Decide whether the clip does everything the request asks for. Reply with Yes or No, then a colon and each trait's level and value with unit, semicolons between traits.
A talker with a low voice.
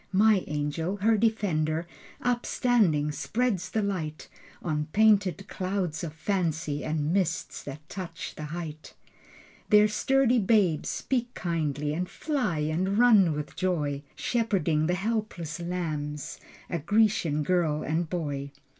No: medium, 175 Hz